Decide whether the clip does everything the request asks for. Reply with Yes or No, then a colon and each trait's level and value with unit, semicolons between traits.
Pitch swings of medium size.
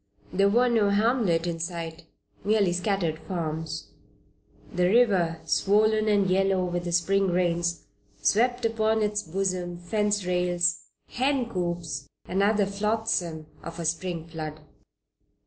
Yes: average, 3.6 semitones